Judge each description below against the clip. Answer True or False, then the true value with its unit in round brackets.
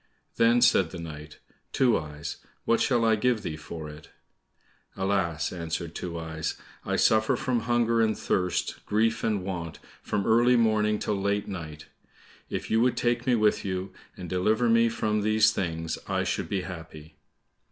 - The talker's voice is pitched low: True (100 Hz)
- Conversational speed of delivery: True (165 wpm)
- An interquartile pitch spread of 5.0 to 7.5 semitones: True (5.4 semitones)